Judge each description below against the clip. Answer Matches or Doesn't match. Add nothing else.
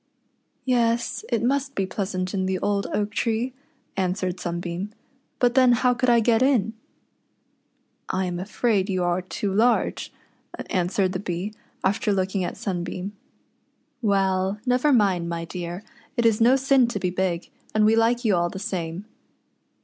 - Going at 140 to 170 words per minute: Matches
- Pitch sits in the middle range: Doesn't match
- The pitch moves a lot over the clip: Doesn't match